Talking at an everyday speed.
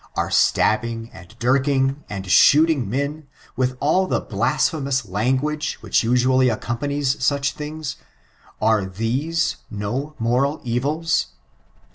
No: slow, 120 wpm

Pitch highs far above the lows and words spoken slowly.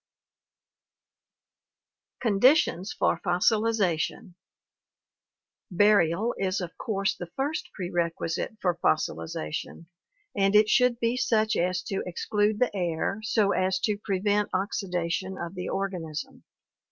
No: average, 3.5 semitones; slow, 105 wpm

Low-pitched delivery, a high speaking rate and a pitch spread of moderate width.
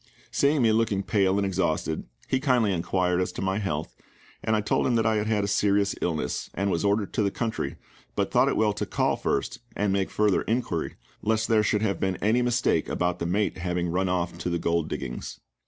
Yes: low, 100 Hz; fast, 220 wpm; average, 3.4 semitones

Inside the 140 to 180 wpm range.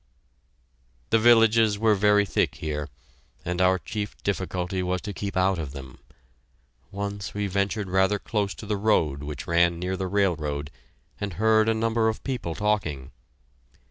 Yes: average, 155 wpm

